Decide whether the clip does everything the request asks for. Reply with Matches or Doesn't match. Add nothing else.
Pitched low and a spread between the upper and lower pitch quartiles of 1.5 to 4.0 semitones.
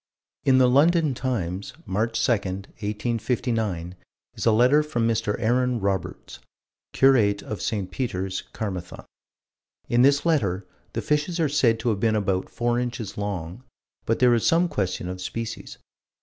Doesn't match